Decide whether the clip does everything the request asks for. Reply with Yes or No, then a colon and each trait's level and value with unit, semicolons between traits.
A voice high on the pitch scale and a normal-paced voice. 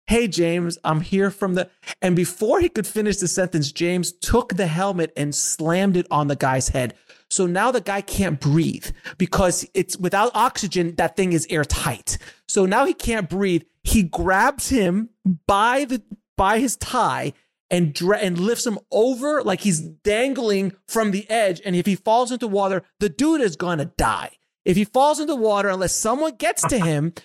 Yes: high, 195 Hz; average, 185 wpm